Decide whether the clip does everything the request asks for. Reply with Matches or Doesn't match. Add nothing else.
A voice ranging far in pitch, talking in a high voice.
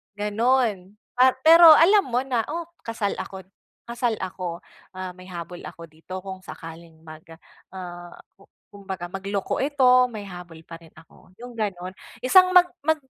Matches